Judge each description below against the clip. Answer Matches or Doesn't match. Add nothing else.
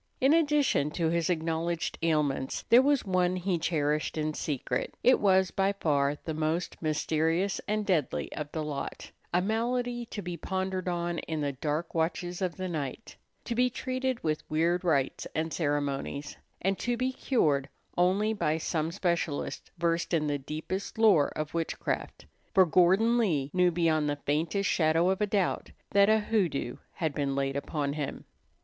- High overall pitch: Doesn't match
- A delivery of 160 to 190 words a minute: Matches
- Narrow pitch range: Doesn't match